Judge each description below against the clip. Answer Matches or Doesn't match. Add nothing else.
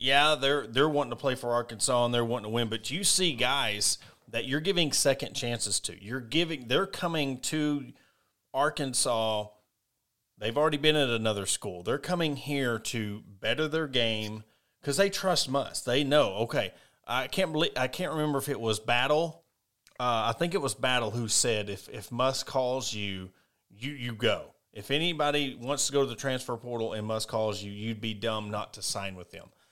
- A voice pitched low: Matches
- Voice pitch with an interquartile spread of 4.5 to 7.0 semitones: Matches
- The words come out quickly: Doesn't match